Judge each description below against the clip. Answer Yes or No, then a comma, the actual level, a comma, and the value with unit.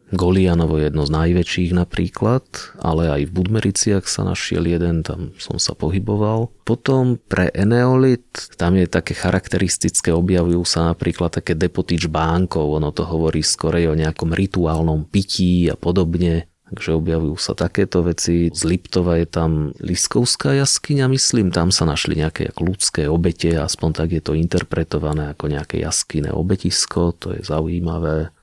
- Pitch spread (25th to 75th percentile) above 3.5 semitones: No, average, 2.7 semitones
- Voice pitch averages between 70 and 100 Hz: Yes, very low, 85 Hz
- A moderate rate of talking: Yes, average, 150 wpm